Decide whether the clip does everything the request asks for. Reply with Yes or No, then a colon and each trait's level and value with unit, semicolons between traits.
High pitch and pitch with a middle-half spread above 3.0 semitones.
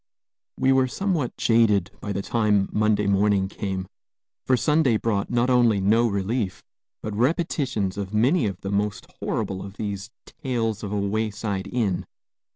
No: low, 105 Hz; average, 3.4 semitones